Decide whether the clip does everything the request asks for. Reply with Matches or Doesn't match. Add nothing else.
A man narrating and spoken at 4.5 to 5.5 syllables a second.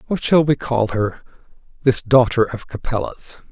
Matches